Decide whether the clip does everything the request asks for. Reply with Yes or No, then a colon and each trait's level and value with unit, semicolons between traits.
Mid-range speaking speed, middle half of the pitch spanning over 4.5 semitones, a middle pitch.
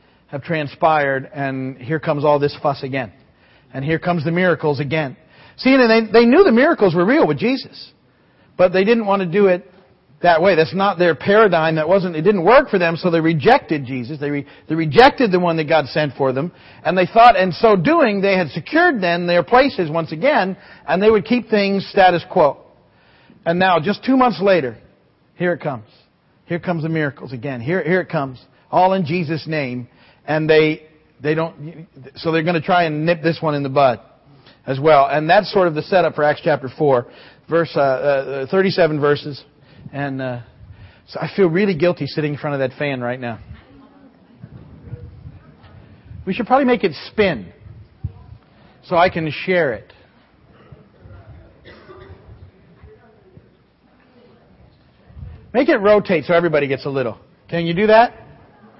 Yes: average, 180 wpm; average, 4.9 semitones; medium, 160 Hz